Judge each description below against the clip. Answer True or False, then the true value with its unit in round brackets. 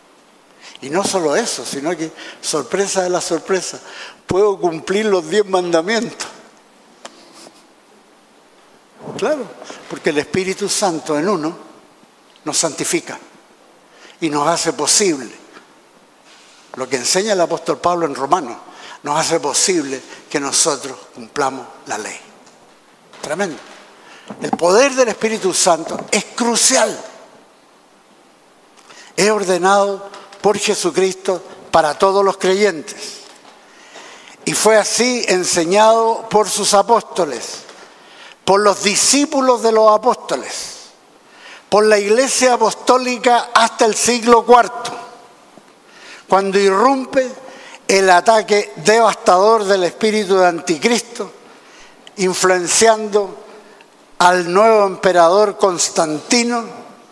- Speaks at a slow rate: True (100 wpm)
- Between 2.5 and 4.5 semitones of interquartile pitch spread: True (3.7 semitones)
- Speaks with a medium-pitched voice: False (205 Hz)